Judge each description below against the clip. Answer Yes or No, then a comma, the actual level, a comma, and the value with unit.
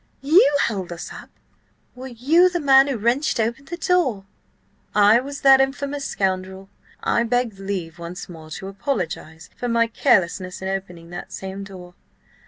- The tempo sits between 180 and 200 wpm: No, average, 160 wpm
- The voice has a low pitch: No, high, 220 Hz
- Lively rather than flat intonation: Yes, wide, 6.2 semitones